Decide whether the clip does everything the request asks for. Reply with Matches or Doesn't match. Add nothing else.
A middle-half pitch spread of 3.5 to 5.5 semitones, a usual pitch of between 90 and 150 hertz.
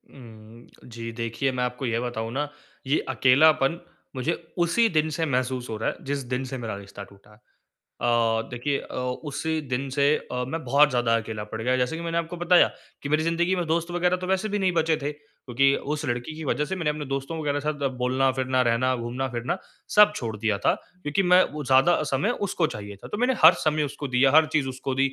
Matches